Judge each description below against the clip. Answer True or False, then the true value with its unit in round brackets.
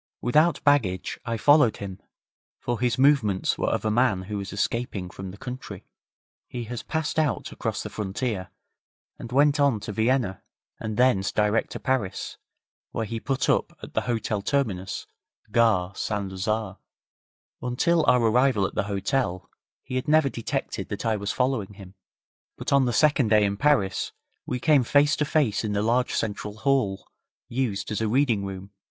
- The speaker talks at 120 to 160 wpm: False (170 wpm)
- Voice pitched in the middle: False (115 Hz)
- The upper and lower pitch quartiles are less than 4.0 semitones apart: False (4.8 semitones)